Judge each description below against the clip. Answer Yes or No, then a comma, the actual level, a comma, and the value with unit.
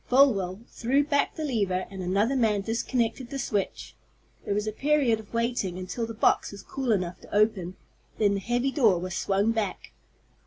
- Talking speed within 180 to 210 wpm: Yes, average, 185 wpm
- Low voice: No, high, 220 Hz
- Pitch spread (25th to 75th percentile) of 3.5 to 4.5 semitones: Yes, average, 4.1 semitones